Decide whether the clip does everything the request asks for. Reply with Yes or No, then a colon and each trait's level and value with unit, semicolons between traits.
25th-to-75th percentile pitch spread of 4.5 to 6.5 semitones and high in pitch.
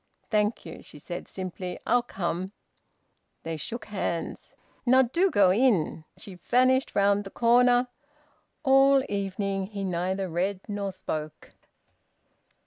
Yes: average, 4.9 semitones; high, 200 Hz